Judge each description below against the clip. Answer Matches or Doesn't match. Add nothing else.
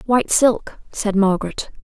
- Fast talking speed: Doesn't match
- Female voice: Matches